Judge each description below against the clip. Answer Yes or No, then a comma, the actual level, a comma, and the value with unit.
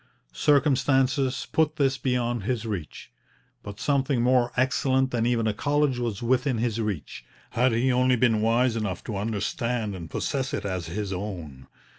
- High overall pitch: No, low, 120 Hz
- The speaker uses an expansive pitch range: No, average, 3.6 semitones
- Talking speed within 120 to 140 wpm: No, average, 160 wpm